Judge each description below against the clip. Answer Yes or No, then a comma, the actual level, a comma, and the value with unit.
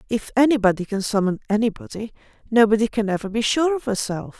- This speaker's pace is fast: No, average, 165 wpm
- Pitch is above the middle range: Yes, high, 220 Hz